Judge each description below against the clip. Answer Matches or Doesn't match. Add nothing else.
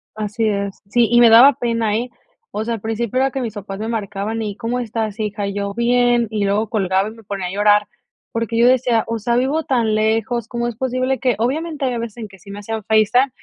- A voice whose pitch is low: Doesn't match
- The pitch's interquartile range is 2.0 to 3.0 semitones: Matches